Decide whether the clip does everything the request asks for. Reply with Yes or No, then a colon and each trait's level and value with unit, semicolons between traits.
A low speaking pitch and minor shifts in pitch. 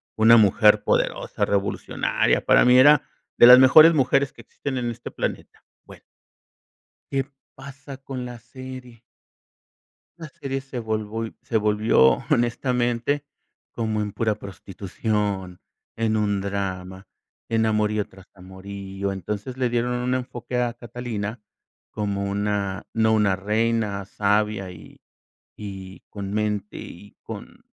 No: low, 110 Hz; average, 3.6 semitones